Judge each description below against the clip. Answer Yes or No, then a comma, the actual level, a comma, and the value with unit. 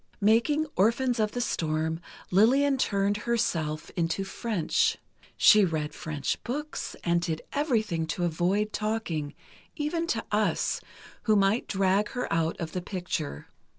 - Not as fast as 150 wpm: Yes, slow, 135 wpm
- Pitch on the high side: Yes, high, 200 Hz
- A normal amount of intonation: No, wide, 6.2 semitones